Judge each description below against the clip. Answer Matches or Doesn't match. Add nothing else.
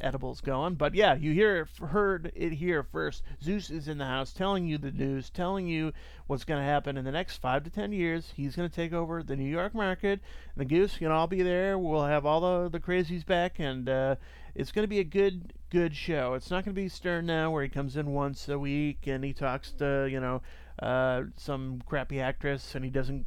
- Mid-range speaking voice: Matches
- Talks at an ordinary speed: Doesn't match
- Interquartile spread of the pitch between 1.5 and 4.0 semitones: Doesn't match